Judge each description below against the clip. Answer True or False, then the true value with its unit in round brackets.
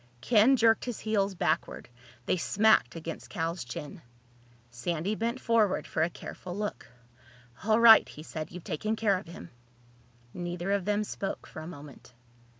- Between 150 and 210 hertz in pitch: True (185 Hz)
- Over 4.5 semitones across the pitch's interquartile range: True (4.9 semitones)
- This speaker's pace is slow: False (155 wpm)